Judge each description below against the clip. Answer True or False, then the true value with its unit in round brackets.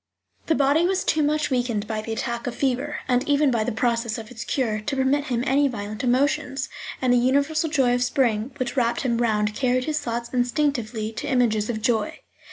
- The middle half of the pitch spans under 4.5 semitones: True (3.4 semitones)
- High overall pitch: True (245 Hz)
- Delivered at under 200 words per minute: False (205 wpm)